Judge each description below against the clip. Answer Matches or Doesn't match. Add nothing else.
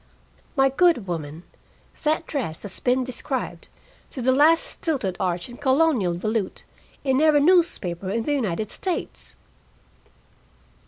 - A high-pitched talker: Matches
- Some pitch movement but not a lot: Doesn't match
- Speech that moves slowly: Matches